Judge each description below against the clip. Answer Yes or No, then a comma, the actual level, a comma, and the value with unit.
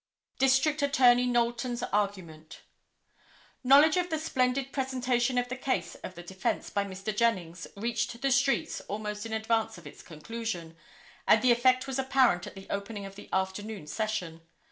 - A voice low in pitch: No, high, 235 Hz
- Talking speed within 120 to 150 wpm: No, average, 160 wpm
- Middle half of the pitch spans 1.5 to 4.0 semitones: No, average, 4.7 semitones